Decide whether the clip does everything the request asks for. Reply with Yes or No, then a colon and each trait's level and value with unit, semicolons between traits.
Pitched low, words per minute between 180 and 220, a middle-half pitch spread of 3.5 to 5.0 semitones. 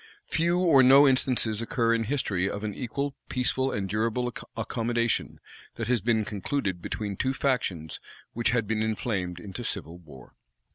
No: low, 115 Hz; average, 155 wpm; average, 4.0 semitones